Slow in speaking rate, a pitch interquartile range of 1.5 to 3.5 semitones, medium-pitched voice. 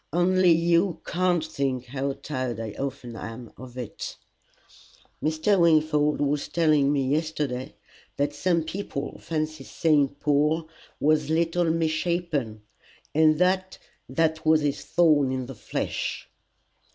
Yes: slow, 125 wpm; average, 3.2 semitones; medium, 155 Hz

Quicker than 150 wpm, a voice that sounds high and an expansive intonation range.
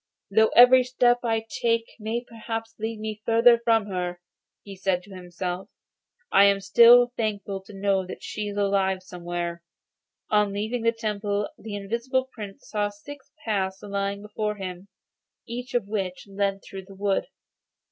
No: average, 160 wpm; high, 205 Hz; average, 2.7 semitones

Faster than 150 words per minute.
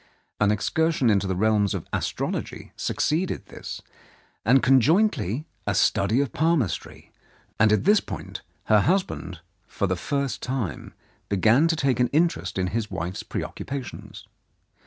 No: average, 140 wpm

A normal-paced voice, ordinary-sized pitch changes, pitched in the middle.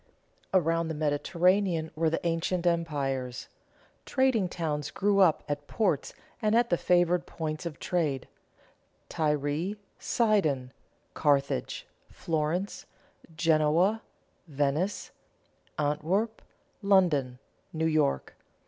No: slow, 95 wpm; average, 3.8 semitones; medium, 165 Hz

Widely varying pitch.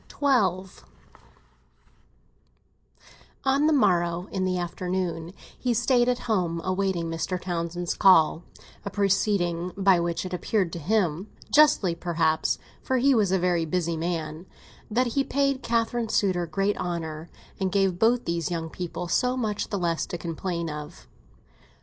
No: average, 4.0 semitones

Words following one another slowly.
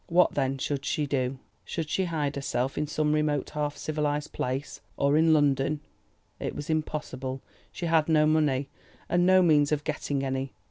No: average, 175 wpm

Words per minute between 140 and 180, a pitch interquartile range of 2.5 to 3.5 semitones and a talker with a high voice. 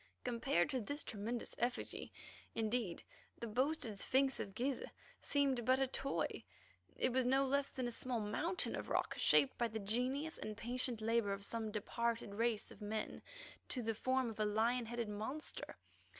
Yes: average, 170 wpm; average, 3.1 semitones; high, 235 Hz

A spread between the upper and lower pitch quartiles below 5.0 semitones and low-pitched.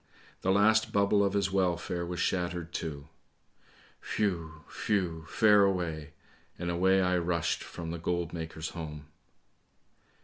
Yes: average, 2.8 semitones; very low, 85 Hz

